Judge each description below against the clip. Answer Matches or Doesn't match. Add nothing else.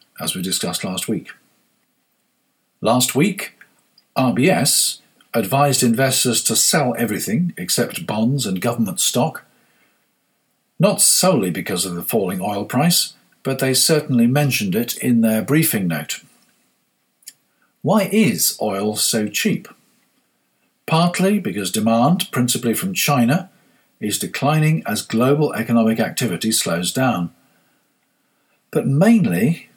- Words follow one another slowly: Matches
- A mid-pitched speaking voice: Matches